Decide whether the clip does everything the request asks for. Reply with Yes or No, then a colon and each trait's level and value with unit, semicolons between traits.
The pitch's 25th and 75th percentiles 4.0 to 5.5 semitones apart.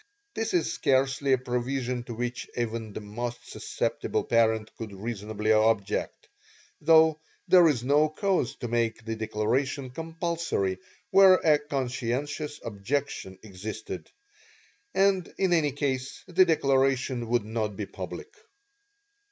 Yes: average, 5.1 semitones